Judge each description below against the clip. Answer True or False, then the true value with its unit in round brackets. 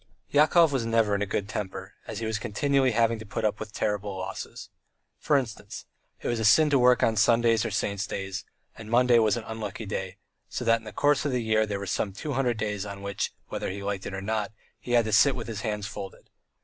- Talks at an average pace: False (240 wpm)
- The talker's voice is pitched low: True (110 Hz)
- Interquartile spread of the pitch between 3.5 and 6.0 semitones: False (2.7 semitones)